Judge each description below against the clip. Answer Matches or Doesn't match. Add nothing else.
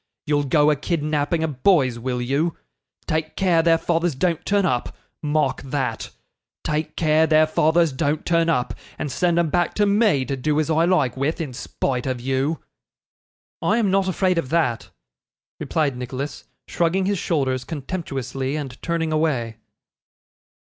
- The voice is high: Doesn't match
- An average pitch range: Matches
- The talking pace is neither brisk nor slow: Matches